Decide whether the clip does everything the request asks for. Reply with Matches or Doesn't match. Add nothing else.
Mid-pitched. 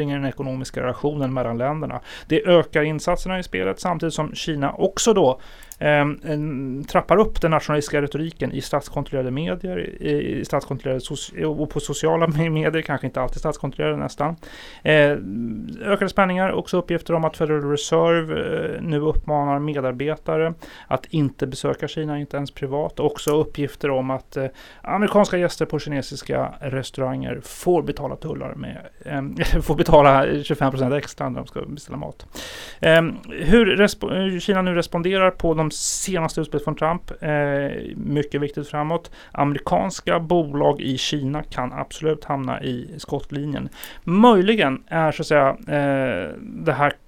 Matches